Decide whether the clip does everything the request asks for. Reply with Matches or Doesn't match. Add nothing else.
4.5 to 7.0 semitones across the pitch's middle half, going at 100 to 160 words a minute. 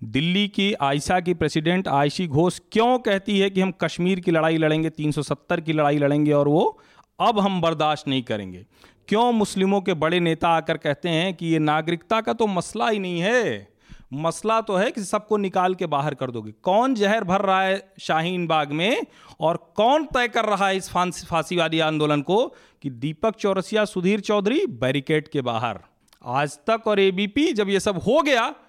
Doesn't match